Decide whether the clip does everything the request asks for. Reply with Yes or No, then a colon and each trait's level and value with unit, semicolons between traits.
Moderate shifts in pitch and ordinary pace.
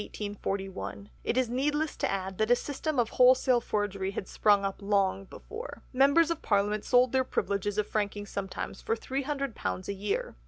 Yes: average, 4.6 semitones; average, 165 wpm